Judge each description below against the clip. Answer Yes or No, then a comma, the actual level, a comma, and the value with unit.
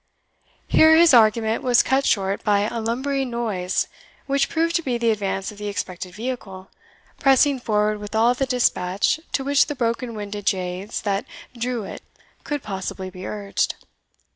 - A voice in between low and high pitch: No, high, 225 Hz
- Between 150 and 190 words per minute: Yes, average, 165 wpm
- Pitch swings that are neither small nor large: Yes, average, 4.3 semitones